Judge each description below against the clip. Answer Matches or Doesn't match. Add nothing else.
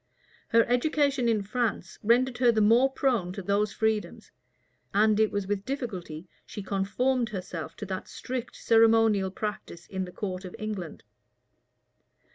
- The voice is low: Doesn't match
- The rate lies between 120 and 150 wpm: Matches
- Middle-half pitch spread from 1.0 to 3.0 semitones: Doesn't match